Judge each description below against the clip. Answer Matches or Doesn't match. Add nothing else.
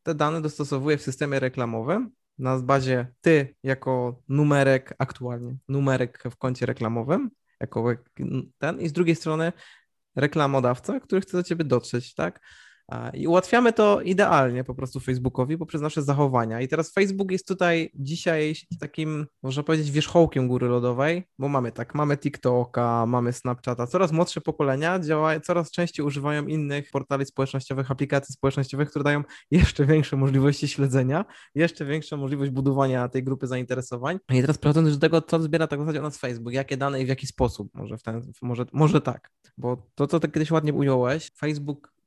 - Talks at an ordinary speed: Doesn't match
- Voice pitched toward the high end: Doesn't match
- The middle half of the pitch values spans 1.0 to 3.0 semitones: Doesn't match